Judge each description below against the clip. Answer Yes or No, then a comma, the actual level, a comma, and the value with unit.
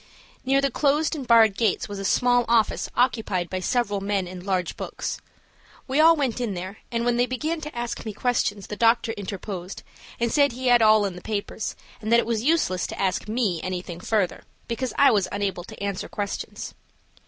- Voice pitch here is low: No, high, 220 Hz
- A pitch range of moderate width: Yes, average, 3.9 semitones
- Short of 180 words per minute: No, average, 200 wpm